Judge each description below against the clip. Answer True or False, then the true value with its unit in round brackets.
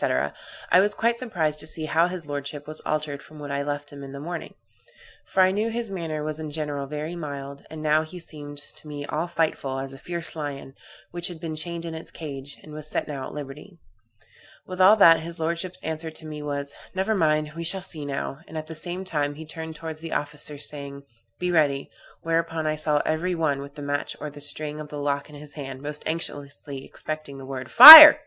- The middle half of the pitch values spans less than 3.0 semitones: True (2.5 semitones)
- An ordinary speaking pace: False (220 wpm)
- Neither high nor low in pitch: True (155 Hz)